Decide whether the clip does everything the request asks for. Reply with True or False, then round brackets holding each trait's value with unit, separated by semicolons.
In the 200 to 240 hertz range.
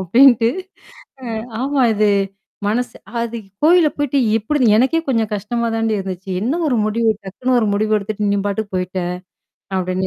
True (220 Hz)